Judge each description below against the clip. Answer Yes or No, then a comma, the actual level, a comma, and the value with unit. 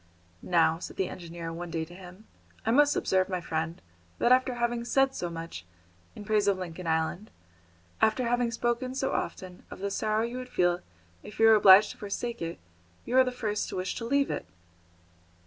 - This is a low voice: No, high, 205 Hz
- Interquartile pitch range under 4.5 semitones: No, wide, 5.4 semitones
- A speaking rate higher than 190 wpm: Yes, average, 200 wpm